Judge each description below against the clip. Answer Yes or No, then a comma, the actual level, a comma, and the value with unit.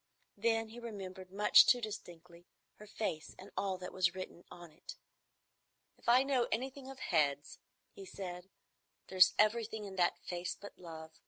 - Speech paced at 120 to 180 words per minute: Yes, average, 160 wpm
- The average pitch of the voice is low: No, high, 190 Hz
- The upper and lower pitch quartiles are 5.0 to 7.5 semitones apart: No, average, 4.1 semitones